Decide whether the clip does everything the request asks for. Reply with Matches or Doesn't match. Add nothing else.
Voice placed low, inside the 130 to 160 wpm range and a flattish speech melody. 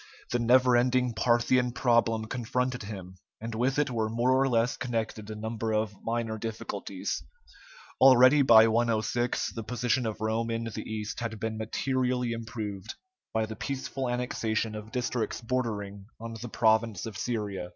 Matches